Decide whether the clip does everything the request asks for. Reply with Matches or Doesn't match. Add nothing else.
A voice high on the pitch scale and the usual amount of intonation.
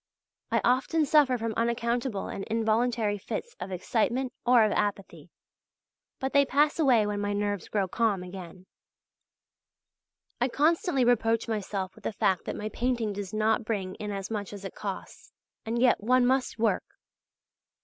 Matches